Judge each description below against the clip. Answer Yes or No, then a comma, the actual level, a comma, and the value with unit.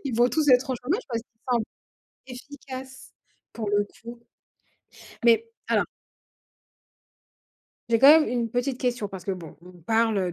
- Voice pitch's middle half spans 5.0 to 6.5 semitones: No, average, 2.8 semitones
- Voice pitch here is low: No, high, 240 Hz